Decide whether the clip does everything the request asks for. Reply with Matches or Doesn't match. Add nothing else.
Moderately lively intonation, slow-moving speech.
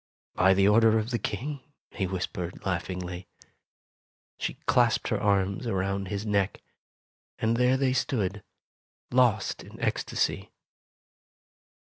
Matches